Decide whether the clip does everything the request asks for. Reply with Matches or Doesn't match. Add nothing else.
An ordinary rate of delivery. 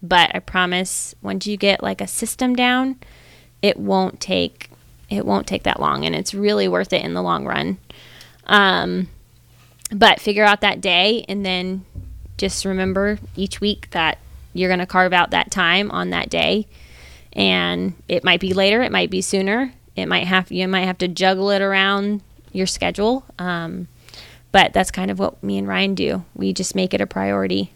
Matches